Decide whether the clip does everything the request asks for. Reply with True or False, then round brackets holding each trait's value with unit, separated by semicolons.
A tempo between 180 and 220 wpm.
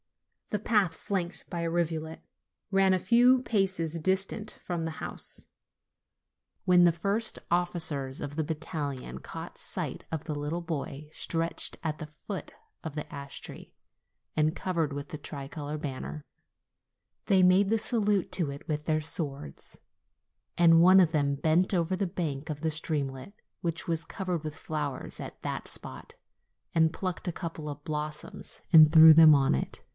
False (160 wpm)